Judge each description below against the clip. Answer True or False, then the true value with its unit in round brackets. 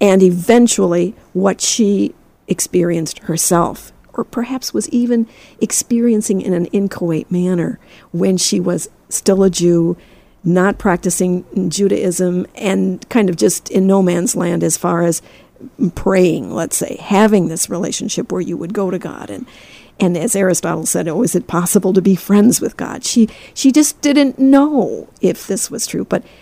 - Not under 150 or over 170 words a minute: True (160 wpm)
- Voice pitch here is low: False (190 Hz)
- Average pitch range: True (3.5 semitones)